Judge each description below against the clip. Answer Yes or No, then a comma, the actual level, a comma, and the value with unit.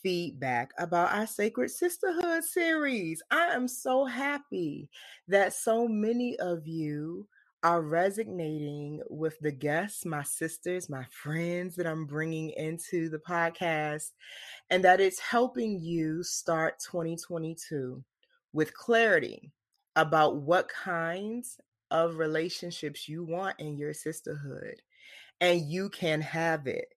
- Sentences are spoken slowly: Yes, slow, 120 wpm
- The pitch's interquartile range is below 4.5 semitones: No, average, 4.8 semitones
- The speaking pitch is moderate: Yes, medium, 170 Hz